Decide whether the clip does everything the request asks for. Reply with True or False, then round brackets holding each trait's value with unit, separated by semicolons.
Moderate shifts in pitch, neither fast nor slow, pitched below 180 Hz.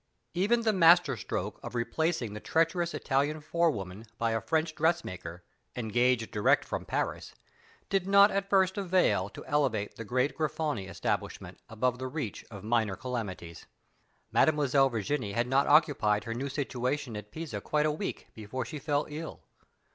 False (6.2 semitones; 155 wpm; 135 Hz)